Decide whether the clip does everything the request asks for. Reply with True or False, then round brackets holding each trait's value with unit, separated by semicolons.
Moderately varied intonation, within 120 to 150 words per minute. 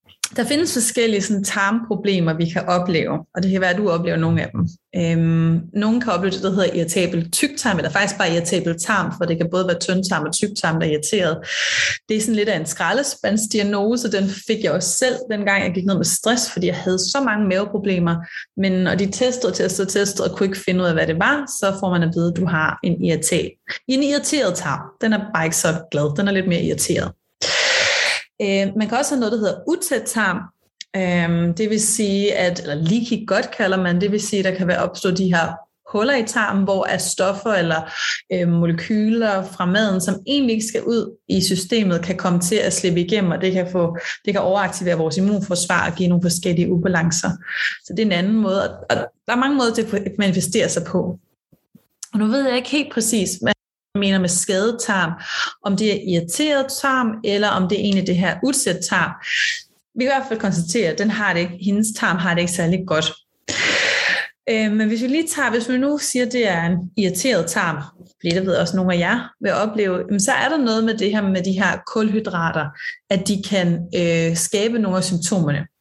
False (3.7 semitones; 220 wpm)